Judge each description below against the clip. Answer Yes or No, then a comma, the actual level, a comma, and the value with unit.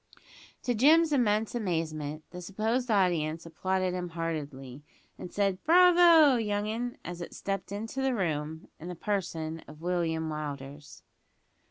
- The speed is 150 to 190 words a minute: No, average, 140 wpm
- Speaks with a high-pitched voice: No, medium, 180 Hz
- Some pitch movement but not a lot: No, wide, 5.8 semitones